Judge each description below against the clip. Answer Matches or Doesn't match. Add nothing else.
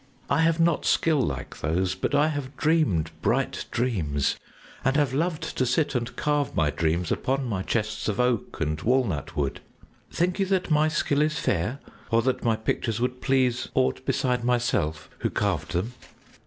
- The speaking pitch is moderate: Doesn't match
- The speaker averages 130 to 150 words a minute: Doesn't match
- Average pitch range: Doesn't match